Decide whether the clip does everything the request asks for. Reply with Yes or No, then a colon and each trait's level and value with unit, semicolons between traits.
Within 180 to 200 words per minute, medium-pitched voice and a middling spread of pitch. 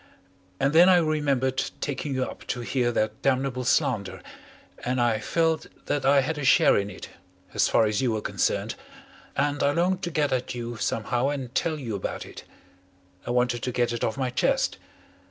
No: average, 190 wpm; low, 130 Hz; average, 3.2 semitones